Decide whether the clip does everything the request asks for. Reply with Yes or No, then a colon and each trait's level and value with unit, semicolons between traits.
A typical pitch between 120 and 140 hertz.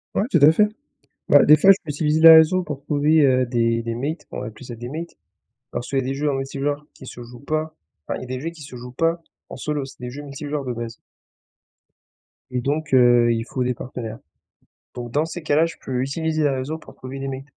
Yes: low, 135 Hz